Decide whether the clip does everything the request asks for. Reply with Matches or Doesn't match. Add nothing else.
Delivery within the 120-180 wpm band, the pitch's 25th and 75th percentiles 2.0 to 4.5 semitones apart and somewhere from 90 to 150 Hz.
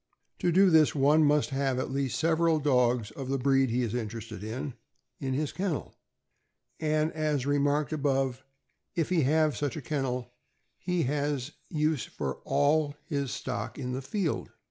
Matches